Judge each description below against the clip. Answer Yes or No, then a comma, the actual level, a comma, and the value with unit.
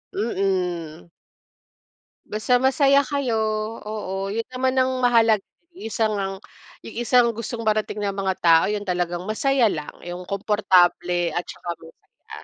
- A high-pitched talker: Yes, high, 210 Hz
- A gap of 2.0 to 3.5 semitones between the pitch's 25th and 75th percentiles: No, average, 4.7 semitones